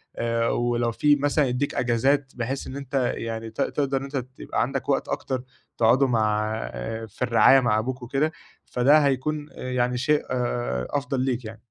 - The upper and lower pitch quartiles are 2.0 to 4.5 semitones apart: Yes, average, 2.9 semitones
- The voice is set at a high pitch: No, low, 125 Hz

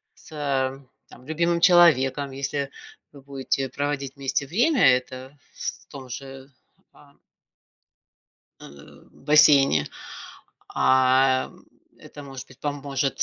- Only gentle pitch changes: Yes, narrow, 1.8 semitones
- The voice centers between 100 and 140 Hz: Yes, low, 135 Hz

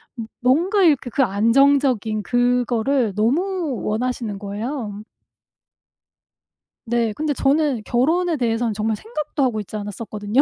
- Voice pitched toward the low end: No, high, 245 Hz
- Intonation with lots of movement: No, average, 4.6 semitones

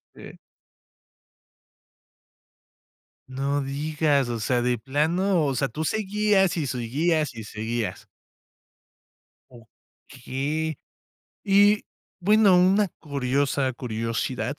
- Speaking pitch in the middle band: Yes, medium, 145 Hz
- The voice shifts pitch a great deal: Yes, wide, 6.0 semitones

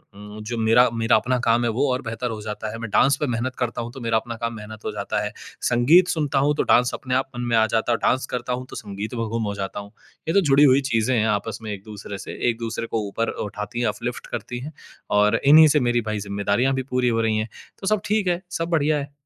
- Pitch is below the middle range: Yes, low, 120 Hz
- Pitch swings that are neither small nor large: Yes, average, 3.2 semitones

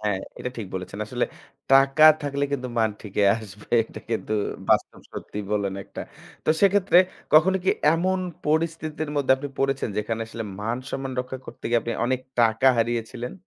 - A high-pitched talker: No, low, 130 Hz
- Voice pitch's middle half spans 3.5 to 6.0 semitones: Yes, average, 4.5 semitones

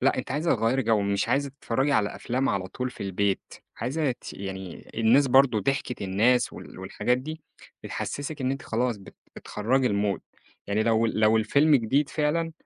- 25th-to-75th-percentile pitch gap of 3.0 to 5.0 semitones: Yes, average, 4.6 semitones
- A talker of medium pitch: No, low, 120 Hz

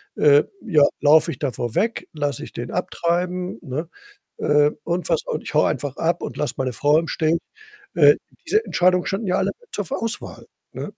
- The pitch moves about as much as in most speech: Yes, average, 3.7 semitones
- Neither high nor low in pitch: Yes, medium, 160 Hz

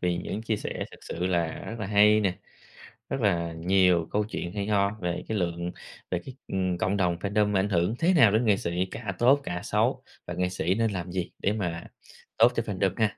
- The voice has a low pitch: Yes, very low, 95 Hz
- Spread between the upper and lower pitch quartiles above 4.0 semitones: No, average, 3.2 semitones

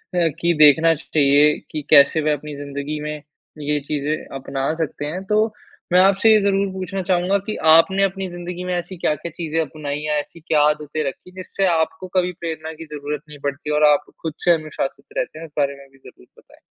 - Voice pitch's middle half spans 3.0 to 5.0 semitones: Yes, average, 3.3 semitones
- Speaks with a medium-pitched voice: Yes, medium, 155 Hz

